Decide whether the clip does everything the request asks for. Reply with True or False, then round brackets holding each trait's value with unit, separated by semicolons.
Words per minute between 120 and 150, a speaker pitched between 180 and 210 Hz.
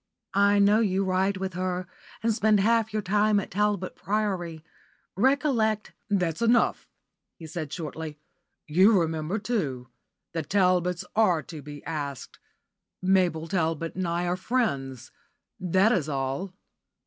True (135 wpm; 185 Hz)